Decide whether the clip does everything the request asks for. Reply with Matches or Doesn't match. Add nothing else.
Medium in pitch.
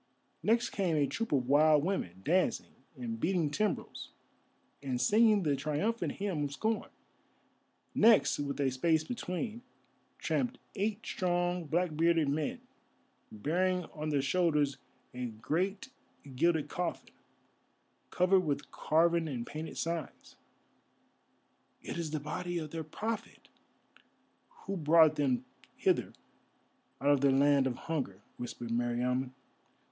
Matches